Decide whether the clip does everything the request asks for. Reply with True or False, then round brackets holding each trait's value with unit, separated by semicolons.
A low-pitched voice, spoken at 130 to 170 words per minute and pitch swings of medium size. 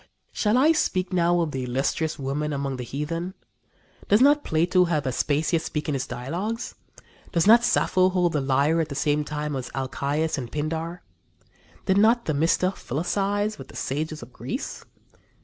False (160 Hz; 165 wpm; 4.7 semitones)